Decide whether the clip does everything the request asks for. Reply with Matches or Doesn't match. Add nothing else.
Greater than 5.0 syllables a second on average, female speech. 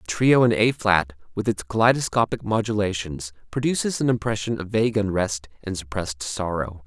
Doesn't match